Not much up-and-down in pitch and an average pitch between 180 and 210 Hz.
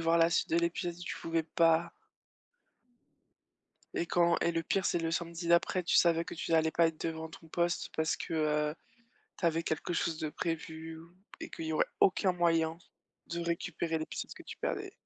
No: narrow, 1.0 semitones; medium, 165 Hz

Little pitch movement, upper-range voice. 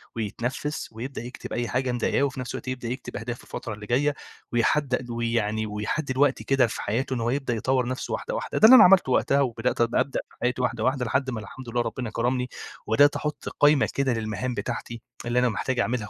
No: narrow, 2.3 semitones; low, 125 Hz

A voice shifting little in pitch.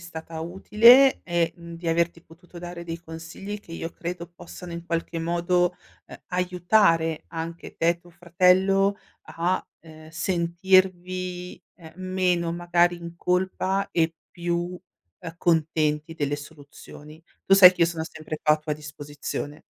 Yes: narrow, 1.8 semitones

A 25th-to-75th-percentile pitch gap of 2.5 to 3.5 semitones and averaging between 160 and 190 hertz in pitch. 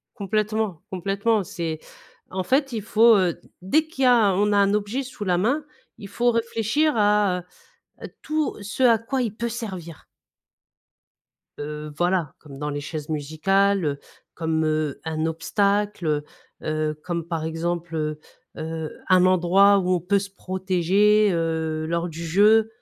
No: average, 4.6 semitones; medium, 185 Hz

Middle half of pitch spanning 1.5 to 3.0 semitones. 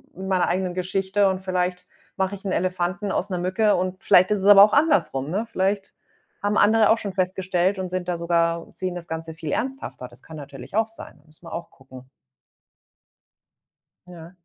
Yes: average, 2.7 semitones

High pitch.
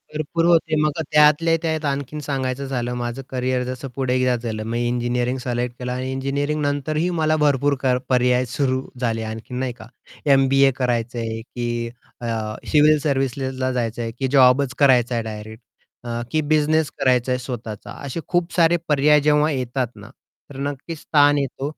No: low, 130 Hz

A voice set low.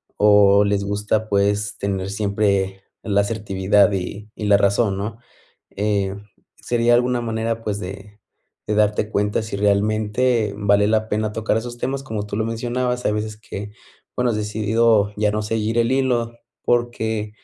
Yes: low, 105 Hz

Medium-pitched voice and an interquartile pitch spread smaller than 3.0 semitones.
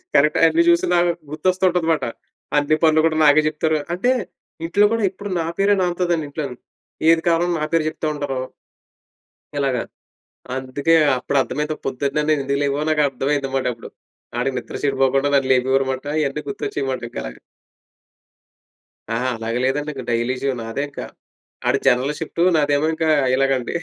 No: medium, 145 Hz; average, 3.3 semitones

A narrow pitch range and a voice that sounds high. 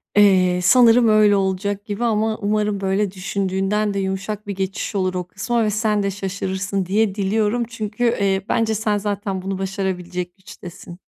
Yes: narrow, 1.9 semitones; high, 200 Hz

